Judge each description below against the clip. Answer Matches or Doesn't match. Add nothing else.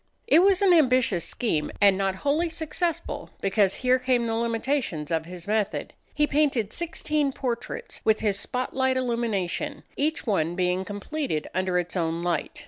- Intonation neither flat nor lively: Doesn't match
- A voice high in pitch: Matches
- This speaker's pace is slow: Doesn't match